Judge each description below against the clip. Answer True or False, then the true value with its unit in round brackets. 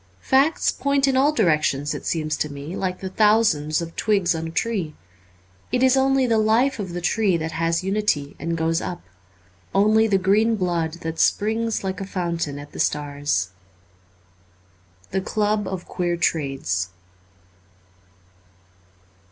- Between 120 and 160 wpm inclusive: True (155 wpm)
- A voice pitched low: False (175 Hz)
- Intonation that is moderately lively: False (6.0 semitones)